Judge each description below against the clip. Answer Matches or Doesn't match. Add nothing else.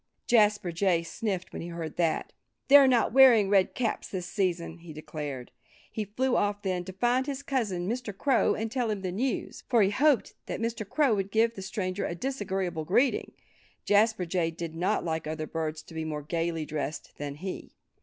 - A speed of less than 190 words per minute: Doesn't match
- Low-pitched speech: Doesn't match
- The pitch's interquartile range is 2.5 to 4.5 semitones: Doesn't match